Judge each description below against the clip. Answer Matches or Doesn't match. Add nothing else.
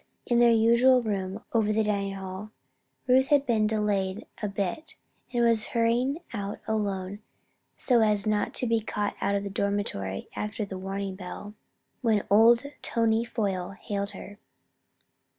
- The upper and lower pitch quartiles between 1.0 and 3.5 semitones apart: Matches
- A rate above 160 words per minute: Doesn't match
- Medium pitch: Doesn't match